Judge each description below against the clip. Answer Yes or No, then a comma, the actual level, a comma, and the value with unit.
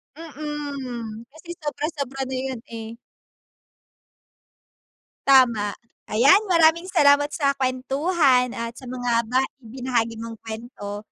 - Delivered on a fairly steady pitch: No, average, 3.9 semitones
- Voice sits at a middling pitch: No, very high, 255 Hz